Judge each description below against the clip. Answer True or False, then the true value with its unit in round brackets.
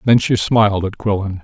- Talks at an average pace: False (210 wpm)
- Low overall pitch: True (105 Hz)